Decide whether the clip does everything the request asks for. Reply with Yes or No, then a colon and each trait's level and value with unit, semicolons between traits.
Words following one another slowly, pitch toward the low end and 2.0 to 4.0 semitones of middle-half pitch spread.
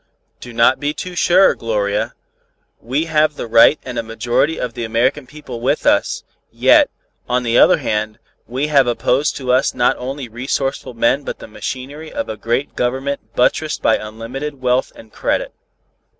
No: average, 170 wpm; low, 125 Hz; average, 3.5 semitones